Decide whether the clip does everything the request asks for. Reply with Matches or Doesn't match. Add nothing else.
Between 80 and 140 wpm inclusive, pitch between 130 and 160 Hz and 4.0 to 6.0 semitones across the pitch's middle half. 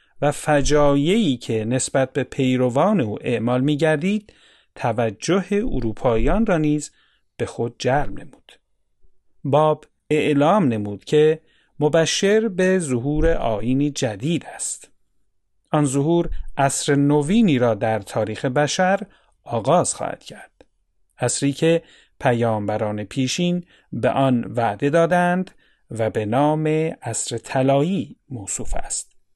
Matches